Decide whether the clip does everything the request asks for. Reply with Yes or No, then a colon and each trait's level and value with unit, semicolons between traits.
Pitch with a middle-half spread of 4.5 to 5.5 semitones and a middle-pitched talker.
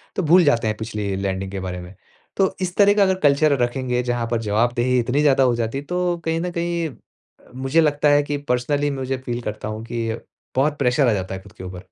No: average, 4.9 semitones; low, 125 Hz